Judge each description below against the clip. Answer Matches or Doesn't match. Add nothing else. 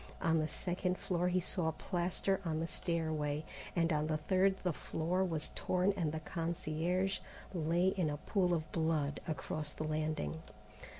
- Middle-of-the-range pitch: Matches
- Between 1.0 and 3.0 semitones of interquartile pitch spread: Matches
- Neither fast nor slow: Matches